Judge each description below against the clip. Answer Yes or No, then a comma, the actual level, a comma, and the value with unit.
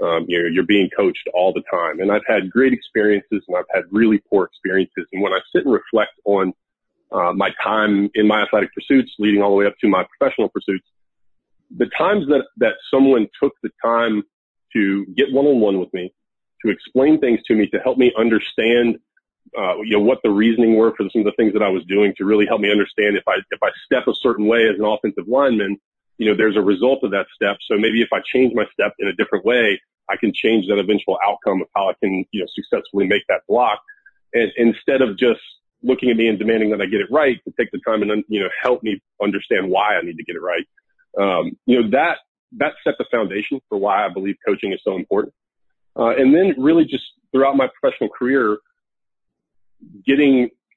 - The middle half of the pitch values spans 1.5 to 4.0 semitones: No, average, 4.4 semitones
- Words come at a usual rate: No, fast, 225 wpm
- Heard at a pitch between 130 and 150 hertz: No, low, 110 Hz